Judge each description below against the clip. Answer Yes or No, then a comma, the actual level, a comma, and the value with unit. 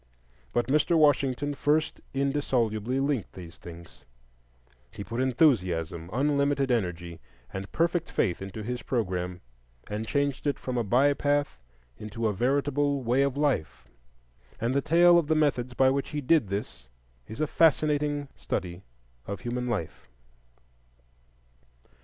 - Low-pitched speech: Yes, low, 130 Hz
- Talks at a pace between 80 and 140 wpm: Yes, slow, 135 wpm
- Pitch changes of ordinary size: No, wide, 6.0 semitones